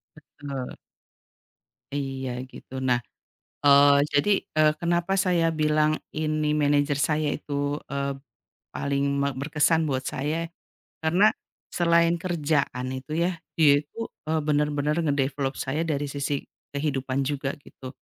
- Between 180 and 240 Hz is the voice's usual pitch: No, medium, 145 Hz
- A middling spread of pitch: No, narrow, 1.9 semitones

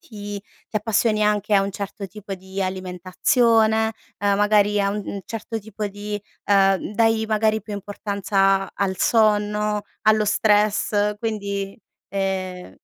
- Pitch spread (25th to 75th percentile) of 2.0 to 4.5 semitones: No, narrow, 1.5 semitones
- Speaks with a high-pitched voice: Yes, high, 205 Hz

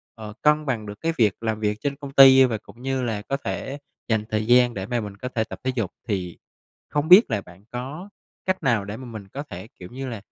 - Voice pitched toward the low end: Yes, low, 120 Hz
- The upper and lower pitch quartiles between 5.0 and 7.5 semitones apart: No, average, 4.4 semitones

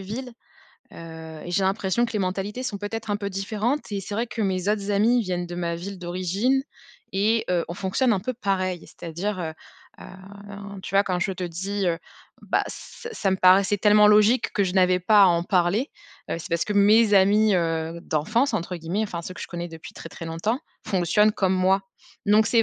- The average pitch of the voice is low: No, high, 195 Hz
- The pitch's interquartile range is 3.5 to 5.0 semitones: No, average, 2.9 semitones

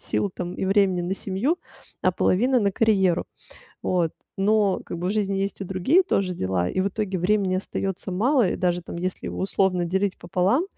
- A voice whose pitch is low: No, high, 190 Hz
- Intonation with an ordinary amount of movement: No, narrow, 2.2 semitones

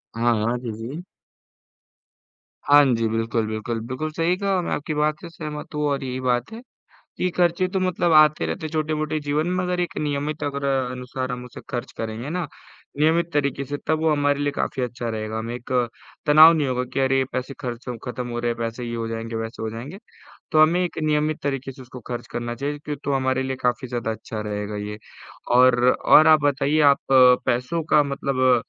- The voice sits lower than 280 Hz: Yes, low, 135 Hz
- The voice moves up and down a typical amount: Yes, average, 4.2 semitones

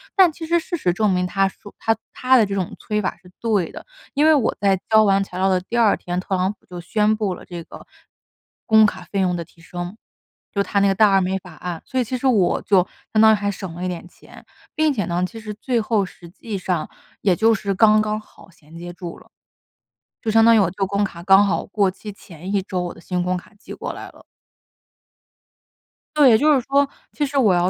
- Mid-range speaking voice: No, high, 200 Hz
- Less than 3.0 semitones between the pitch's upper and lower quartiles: No, average, 3.4 semitones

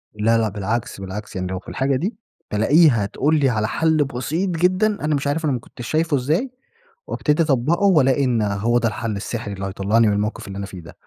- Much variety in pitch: Yes, wide, 6.6 semitones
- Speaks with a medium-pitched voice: No, low, 120 Hz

